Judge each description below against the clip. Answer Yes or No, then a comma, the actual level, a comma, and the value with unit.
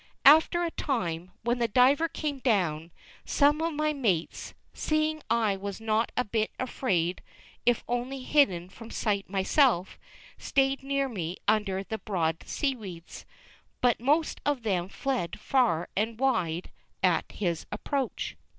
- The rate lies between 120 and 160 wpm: Yes, average, 140 wpm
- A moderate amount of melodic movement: No, wide, 6.3 semitones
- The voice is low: No, high, 230 Hz